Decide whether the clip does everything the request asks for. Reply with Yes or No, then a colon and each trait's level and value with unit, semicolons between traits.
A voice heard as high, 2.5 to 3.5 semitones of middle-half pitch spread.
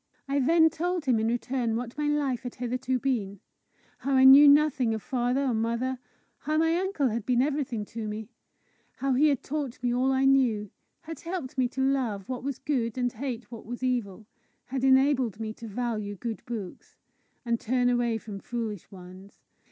Yes: very high, 250 Hz; average, 3.2 semitones